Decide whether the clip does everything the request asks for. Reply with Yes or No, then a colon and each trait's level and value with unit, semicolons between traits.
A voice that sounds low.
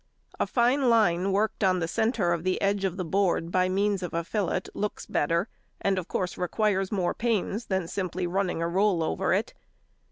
No: high, 190 Hz